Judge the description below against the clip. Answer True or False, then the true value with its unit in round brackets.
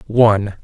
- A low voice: True (105 Hz)